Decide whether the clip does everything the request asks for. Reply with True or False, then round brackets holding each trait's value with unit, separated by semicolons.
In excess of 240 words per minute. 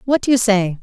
True (290 wpm)